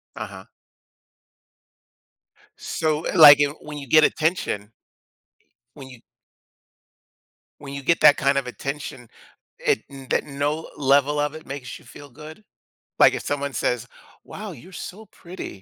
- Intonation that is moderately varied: No, narrow, 2.3 semitones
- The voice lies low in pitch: No, medium, 145 Hz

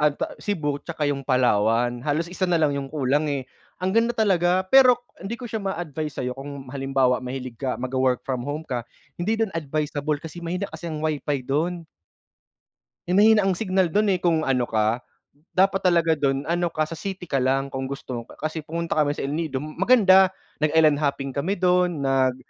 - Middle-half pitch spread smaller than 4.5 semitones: No, average, 4.8 semitones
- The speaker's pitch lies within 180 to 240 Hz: No, medium, 155 Hz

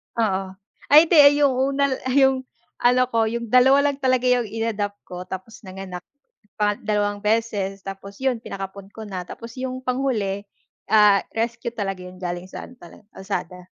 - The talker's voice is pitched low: No, high, 220 Hz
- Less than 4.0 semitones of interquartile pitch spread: No, average, 4.6 semitones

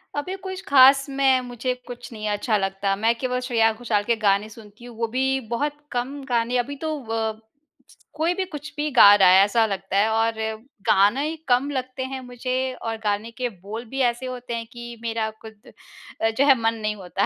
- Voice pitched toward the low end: No, high, 235 Hz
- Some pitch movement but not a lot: Yes, average, 3.3 semitones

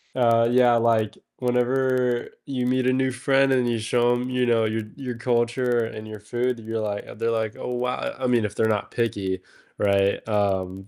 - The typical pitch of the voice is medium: No, low, 120 Hz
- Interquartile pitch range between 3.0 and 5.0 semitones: No, narrow, 2.4 semitones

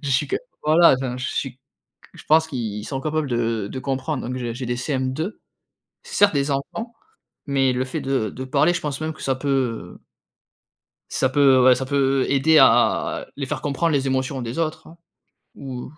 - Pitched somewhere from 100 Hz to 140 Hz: Yes, low, 135 Hz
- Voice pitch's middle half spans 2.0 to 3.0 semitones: Yes, average, 2.7 semitones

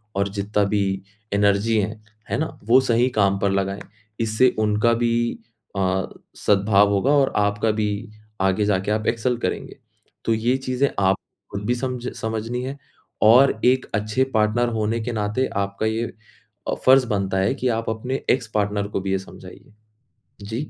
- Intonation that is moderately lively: Yes, average, 3.2 semitones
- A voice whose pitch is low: Yes, low, 110 Hz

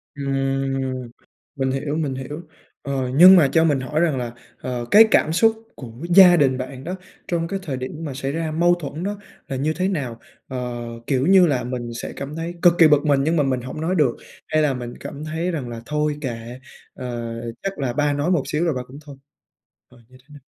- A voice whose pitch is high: No, medium, 145 Hz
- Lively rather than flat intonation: No, average, 4.2 semitones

